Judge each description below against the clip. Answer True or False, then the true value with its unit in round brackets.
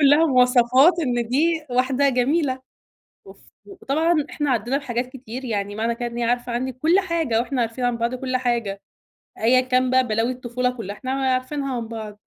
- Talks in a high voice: True (255 Hz)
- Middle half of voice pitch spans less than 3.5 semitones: True (2.4 semitones)